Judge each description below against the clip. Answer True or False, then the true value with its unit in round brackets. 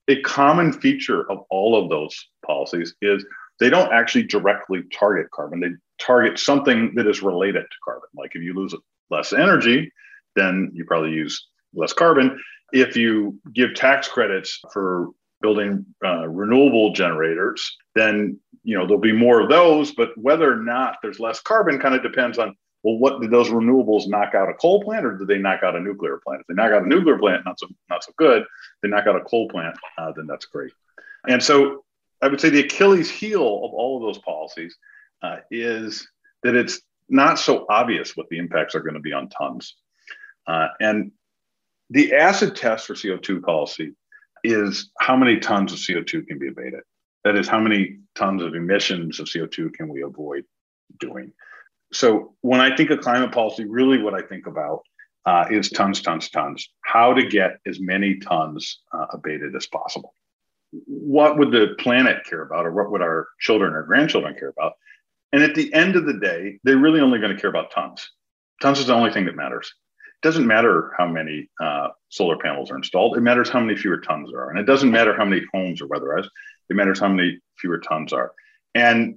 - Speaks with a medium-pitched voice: False (115 Hz)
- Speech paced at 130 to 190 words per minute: False (200 wpm)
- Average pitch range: False (7.2 semitones)